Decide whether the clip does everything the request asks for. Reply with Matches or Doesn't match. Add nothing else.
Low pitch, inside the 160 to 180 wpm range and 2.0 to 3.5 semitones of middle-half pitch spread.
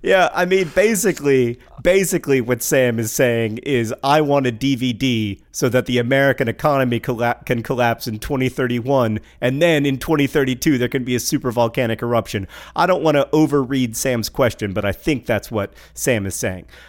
Matches